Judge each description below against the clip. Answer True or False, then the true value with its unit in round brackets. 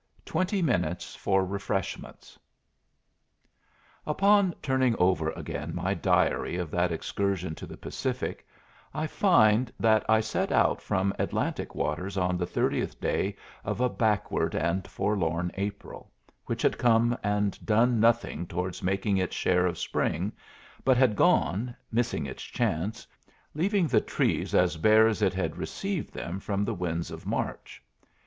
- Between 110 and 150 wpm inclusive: True (145 wpm)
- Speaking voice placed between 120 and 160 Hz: False (100 Hz)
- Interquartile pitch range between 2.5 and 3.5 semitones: False (4.7 semitones)